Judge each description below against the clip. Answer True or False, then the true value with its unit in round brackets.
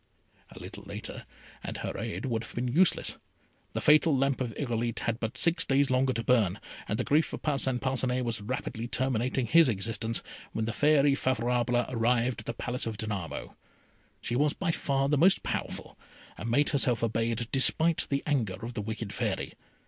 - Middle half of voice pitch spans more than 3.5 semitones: False (3.2 semitones)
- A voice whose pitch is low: True (125 Hz)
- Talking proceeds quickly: False (185 wpm)